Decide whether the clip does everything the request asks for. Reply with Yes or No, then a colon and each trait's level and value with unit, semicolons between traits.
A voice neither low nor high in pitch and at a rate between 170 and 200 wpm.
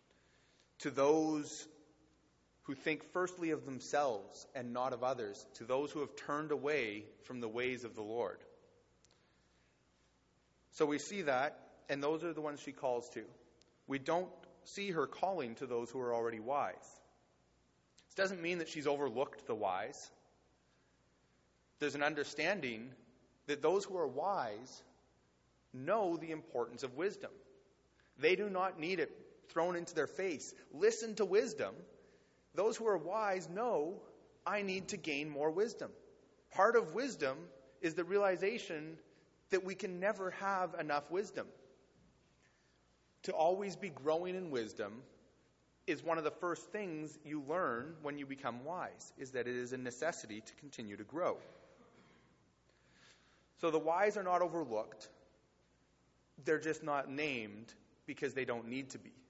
No: medium, 150 Hz; average, 150 wpm